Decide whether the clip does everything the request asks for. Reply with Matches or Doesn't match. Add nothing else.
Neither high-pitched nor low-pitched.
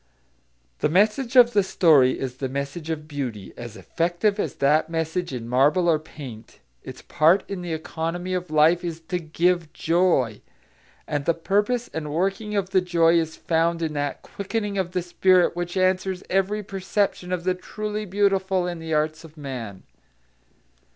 Matches